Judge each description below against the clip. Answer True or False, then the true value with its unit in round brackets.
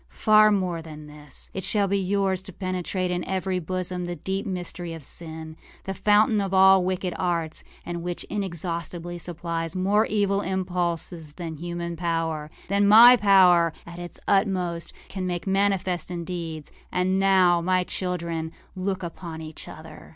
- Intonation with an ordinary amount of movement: False (2.2 semitones)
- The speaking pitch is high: False (180 Hz)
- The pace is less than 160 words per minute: True (150 wpm)